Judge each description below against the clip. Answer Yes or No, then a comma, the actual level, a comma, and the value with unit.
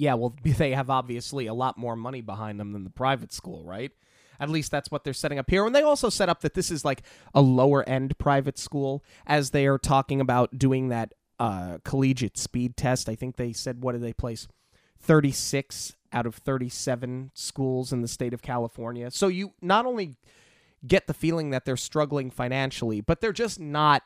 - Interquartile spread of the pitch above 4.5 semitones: No, average, 3.3 semitones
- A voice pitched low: Yes, low, 130 Hz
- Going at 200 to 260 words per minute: Yes, fast, 205 wpm